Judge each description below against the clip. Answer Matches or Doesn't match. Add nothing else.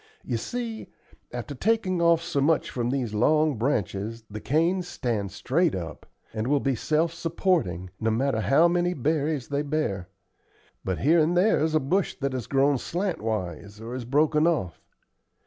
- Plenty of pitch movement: Matches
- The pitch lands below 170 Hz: Matches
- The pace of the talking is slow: Doesn't match